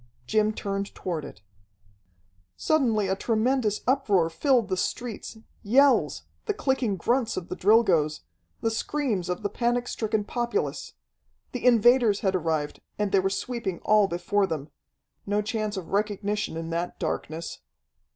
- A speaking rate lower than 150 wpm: Yes, average, 140 wpm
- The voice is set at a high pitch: Yes, high, 210 Hz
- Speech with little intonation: No, average, 4.3 semitones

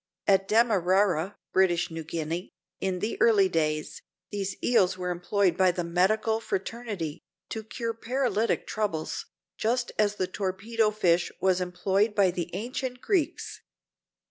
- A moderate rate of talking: No, slow, 130 wpm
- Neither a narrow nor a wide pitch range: Yes, average, 3.7 semitones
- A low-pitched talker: No, high, 195 Hz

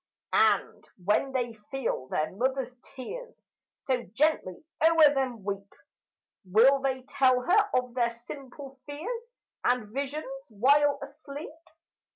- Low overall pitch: No, very high, 265 Hz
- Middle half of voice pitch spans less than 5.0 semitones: Yes, average, 3.3 semitones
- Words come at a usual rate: No, slow, 120 wpm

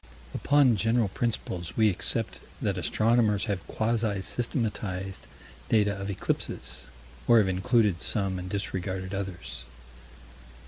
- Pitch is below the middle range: Yes, low, 100 Hz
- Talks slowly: Yes, slow, 110 wpm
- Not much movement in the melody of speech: No, average, 3.2 semitones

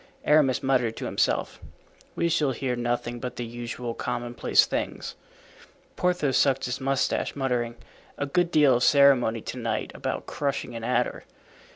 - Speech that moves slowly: No, average, 150 wpm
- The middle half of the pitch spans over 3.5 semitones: No, average, 2.7 semitones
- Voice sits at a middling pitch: No, low, 125 Hz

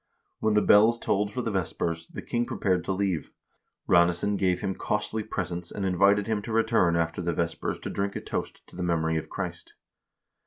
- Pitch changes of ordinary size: Yes, average, 3.4 semitones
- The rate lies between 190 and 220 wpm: Yes, average, 195 wpm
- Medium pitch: No, very low, 95 Hz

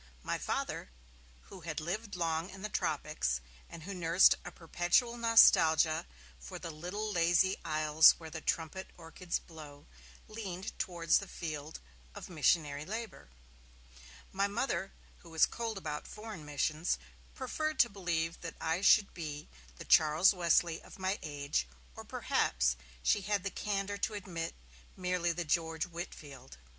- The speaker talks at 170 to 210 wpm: No, average, 145 wpm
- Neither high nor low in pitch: Yes, medium, 170 Hz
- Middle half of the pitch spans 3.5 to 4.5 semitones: Yes, average, 3.8 semitones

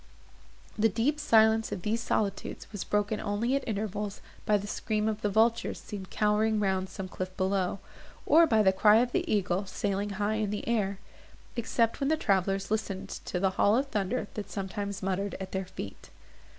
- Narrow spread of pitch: Yes, narrow, 2.2 semitones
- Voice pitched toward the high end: Yes, high, 210 Hz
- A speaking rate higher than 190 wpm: No, average, 180 wpm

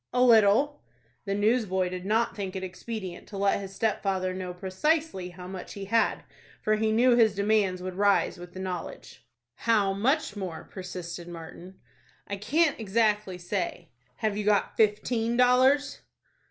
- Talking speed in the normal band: Yes, average, 155 wpm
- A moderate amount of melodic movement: Yes, average, 3.3 semitones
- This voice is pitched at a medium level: No, high, 200 Hz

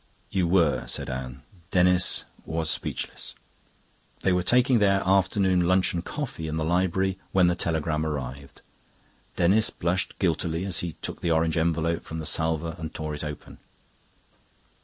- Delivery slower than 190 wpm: Yes, average, 150 wpm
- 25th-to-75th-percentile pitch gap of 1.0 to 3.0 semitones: Yes, average, 2.7 semitones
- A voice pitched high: No, very low, 85 Hz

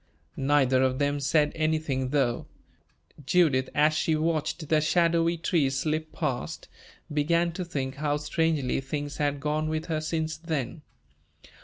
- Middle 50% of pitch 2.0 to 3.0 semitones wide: Yes, narrow, 2.4 semitones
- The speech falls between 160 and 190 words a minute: No, average, 140 wpm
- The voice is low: No, medium, 155 Hz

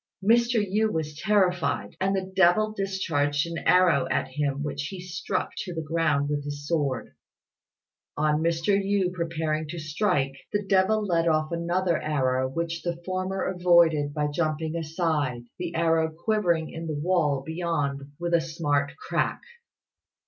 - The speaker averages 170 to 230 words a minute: No, average, 150 wpm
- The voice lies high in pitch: No, medium, 165 Hz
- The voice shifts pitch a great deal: No, average, 3.6 semitones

